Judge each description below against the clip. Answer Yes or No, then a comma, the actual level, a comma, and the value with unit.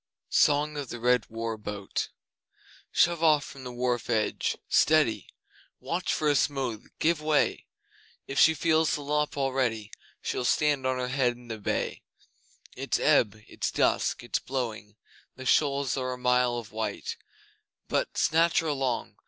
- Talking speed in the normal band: Yes, average, 155 wpm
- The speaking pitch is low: Yes, low, 130 Hz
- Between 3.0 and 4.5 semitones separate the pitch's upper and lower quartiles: Yes, average, 3.8 semitones